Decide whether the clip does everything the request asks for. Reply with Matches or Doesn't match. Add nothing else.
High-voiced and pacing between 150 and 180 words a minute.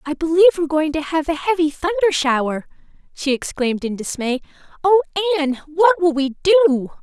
Matches